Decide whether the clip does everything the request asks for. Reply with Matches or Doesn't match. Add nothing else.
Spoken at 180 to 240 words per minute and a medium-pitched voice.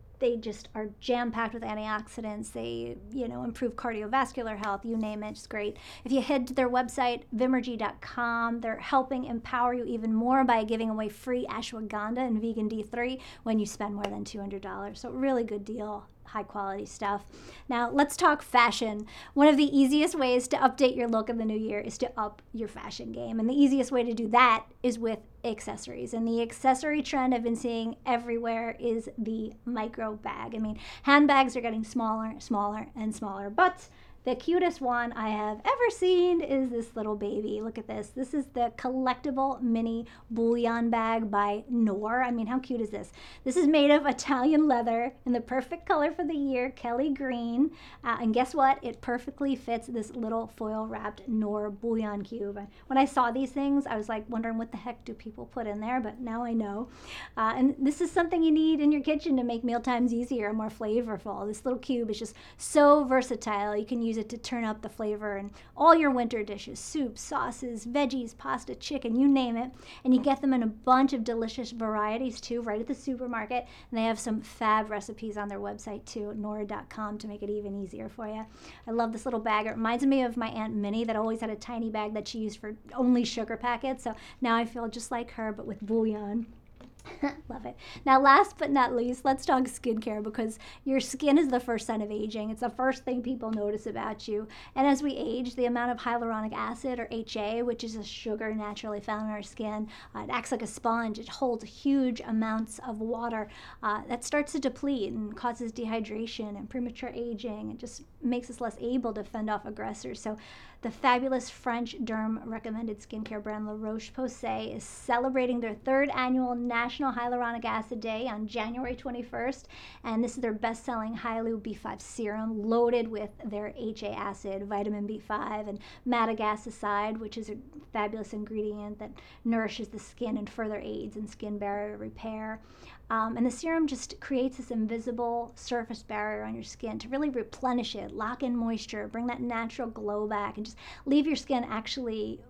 Doesn't match